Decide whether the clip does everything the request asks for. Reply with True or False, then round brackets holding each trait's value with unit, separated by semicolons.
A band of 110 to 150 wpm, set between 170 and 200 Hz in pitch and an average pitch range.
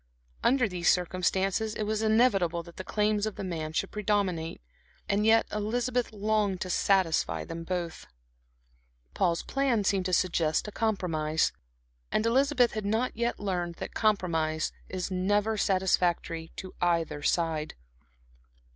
True (140 wpm; 190 Hz; 4.0 semitones)